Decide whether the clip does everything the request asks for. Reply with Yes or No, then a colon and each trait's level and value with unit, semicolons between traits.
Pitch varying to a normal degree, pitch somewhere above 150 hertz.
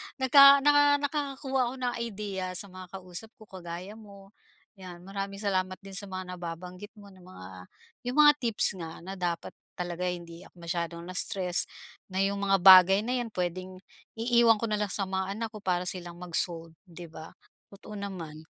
Yes: average, 3.1 semitones; high, 190 Hz